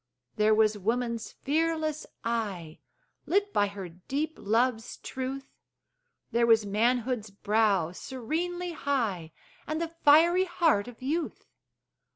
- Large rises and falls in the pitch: Yes, wide, 6.6 semitones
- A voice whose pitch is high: Yes, high, 240 Hz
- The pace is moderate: No, slow, 115 wpm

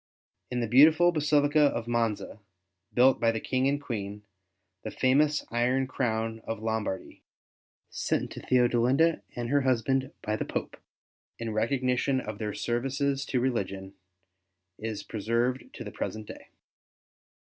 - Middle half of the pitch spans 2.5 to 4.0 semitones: Yes, average, 3.2 semitones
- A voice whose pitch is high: No, low, 120 Hz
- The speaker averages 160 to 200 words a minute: No, slow, 135 wpm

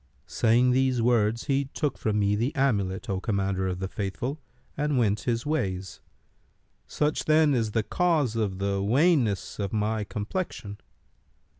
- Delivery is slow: No, average, 150 wpm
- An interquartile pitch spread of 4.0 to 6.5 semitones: Yes, average, 5.3 semitones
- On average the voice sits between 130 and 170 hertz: No, low, 110 Hz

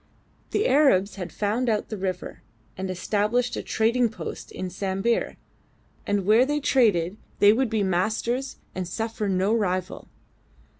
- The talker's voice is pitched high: Yes, high, 210 Hz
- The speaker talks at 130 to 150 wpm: Yes, average, 145 wpm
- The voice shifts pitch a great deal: No, average, 3.9 semitones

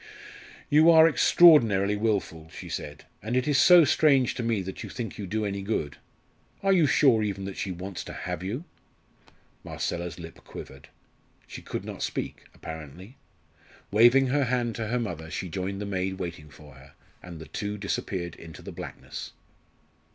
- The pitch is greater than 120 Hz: No, low, 100 Hz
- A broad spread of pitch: Yes, wide, 6.0 semitones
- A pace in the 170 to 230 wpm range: Yes, average, 175 wpm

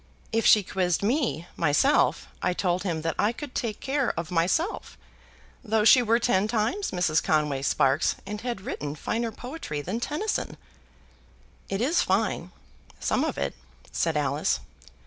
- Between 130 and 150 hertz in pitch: No, high, 205 Hz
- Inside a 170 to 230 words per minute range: No, average, 150 wpm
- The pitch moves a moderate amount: No, wide, 6.4 semitones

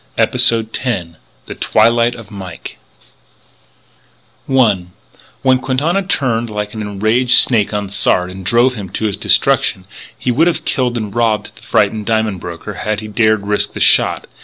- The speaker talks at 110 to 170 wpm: Yes, average, 160 wpm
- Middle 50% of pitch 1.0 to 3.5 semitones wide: Yes, average, 3.1 semitones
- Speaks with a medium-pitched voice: No, low, 110 Hz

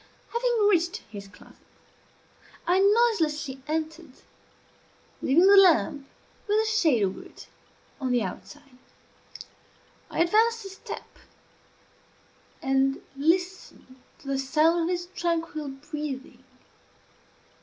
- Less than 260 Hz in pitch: No, very high, 320 Hz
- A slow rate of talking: Yes, slow, 105 wpm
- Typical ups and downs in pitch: No, wide, 5.8 semitones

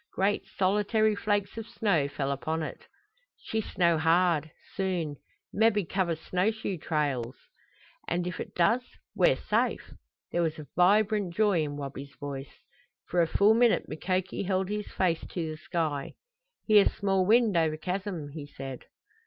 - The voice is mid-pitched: Yes, medium, 180 Hz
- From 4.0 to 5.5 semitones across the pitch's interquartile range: Yes, average, 4.7 semitones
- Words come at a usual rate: Yes, average, 155 wpm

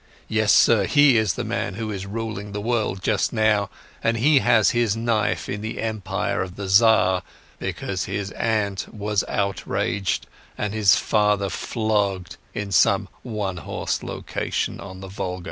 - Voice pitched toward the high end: No, low, 105 Hz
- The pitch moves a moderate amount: No, narrow, 2.2 semitones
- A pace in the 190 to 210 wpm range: No, average, 160 wpm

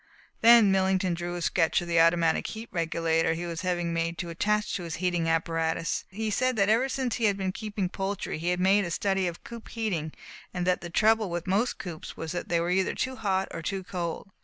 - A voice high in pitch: No, medium, 180 Hz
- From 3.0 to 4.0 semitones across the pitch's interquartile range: Yes, average, 3.5 semitones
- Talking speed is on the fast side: Yes, fast, 230 wpm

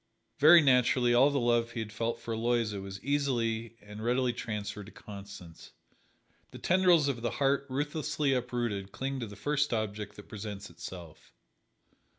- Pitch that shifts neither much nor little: Yes, average, 4.6 semitones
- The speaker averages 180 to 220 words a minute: No, average, 160 wpm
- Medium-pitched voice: No, low, 120 Hz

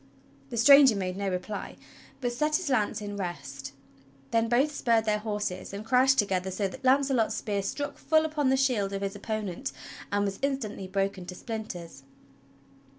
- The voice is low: No, high, 210 Hz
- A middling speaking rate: Yes, average, 170 wpm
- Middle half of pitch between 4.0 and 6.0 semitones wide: Yes, average, 5.0 semitones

